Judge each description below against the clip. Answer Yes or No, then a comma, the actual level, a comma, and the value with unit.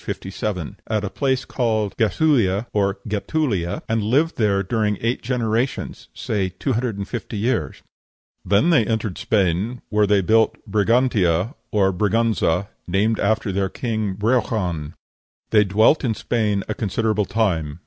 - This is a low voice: Yes, low, 105 Hz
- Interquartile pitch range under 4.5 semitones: Yes, average, 2.9 semitones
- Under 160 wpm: Yes, average, 140 wpm